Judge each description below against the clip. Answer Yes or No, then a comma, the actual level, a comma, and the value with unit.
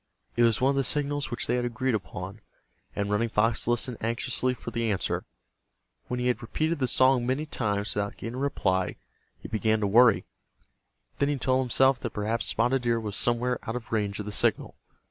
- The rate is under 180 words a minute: No, fast, 205 wpm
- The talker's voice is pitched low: Yes, low, 120 Hz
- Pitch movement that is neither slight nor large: Yes, average, 3.0 semitones